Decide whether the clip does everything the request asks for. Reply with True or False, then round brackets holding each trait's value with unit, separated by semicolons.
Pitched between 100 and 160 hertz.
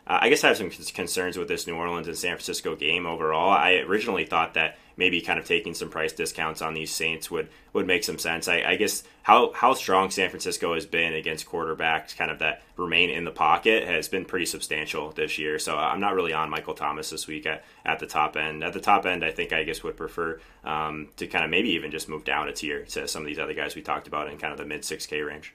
False (80 Hz)